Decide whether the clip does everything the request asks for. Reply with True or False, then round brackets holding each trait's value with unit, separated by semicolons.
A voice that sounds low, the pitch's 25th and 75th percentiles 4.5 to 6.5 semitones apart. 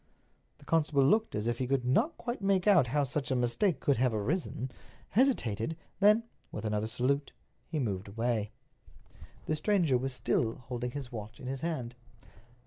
True (130 Hz; 5.6 semitones)